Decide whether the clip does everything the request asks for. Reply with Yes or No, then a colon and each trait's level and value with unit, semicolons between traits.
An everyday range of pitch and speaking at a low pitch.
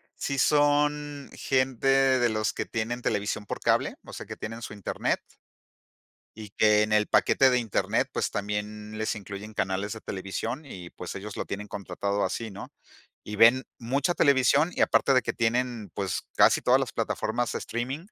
Yes: average, 4.1 semitones; low, 115 Hz